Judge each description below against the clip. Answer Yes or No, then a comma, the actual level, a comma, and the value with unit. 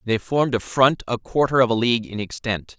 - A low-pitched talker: Yes, low, 120 Hz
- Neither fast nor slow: No, fast, 235 wpm